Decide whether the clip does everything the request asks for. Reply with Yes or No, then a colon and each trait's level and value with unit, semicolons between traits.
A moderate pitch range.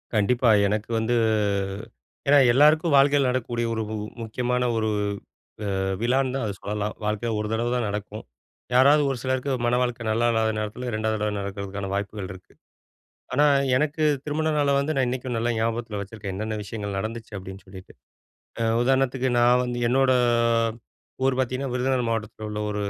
Yes: average, 3.5 semitones